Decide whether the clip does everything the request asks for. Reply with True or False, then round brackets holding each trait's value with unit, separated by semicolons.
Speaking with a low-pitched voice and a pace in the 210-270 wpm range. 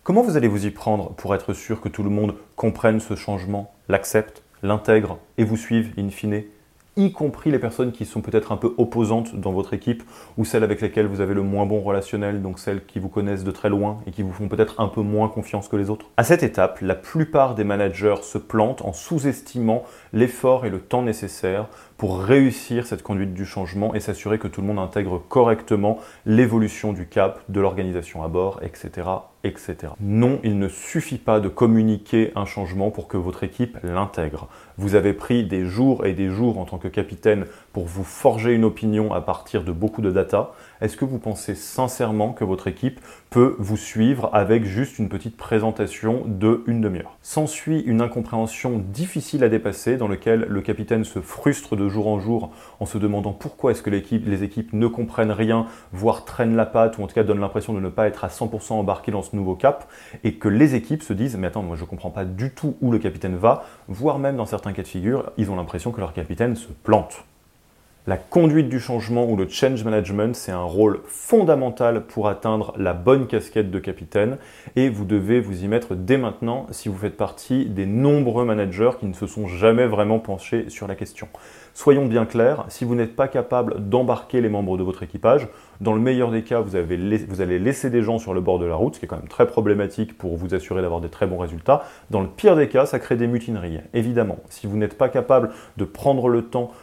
True (105 Hz; 220 wpm)